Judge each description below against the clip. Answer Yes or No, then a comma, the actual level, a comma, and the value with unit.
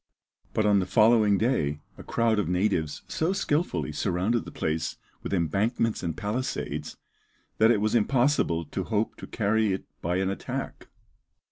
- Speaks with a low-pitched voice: Yes, low, 105 Hz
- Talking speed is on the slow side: No, average, 155 wpm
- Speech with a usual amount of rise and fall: Yes, average, 4.4 semitones